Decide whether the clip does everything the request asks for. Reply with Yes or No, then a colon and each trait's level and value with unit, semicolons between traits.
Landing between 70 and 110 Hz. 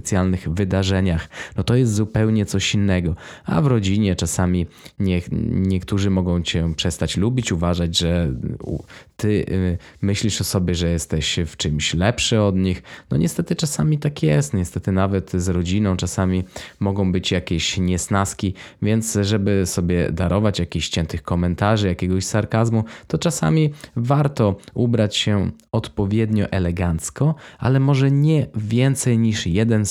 Yes: low, 100 Hz